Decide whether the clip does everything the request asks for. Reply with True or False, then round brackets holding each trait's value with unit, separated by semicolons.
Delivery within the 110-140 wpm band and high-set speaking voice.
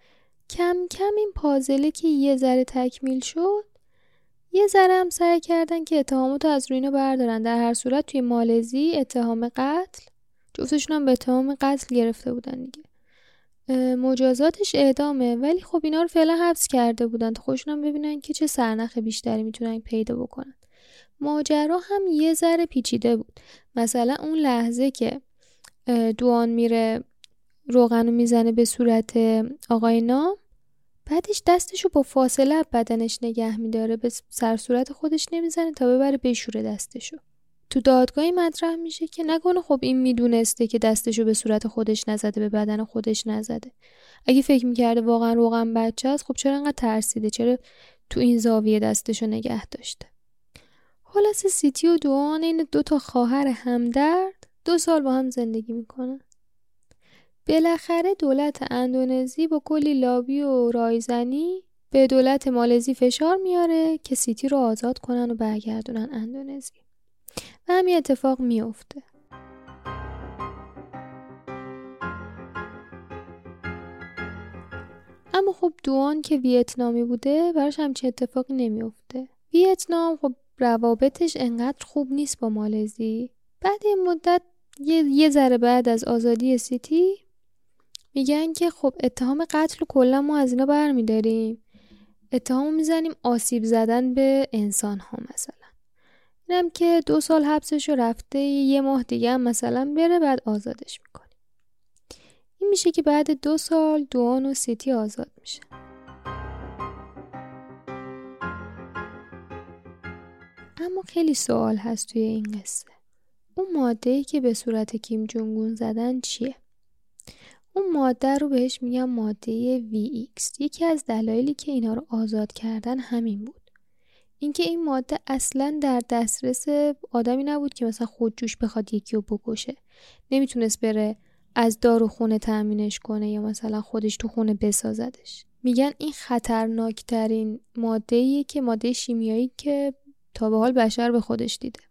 True (135 wpm; 250 Hz)